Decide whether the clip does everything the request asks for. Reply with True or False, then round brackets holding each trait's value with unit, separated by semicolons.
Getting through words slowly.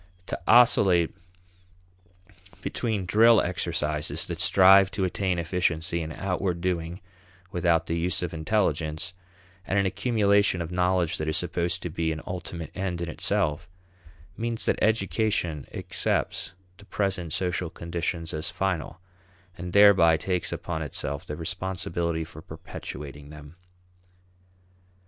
True (125 wpm)